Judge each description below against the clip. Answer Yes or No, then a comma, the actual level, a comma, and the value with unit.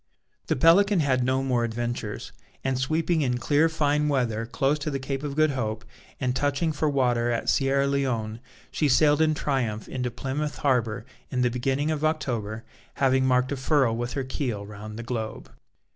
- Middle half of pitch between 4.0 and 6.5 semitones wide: No, average, 3.4 semitones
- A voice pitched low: Yes, low, 130 Hz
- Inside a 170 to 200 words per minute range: Yes, average, 180 wpm